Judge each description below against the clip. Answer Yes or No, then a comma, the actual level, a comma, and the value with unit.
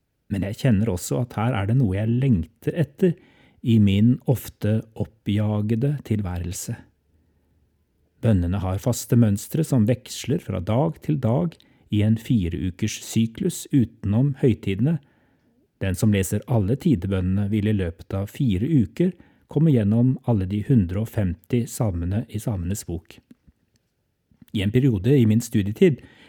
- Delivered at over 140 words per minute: No, slow, 135 wpm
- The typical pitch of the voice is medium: No, low, 110 Hz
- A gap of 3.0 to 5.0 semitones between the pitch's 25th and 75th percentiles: Yes, average, 4.2 semitones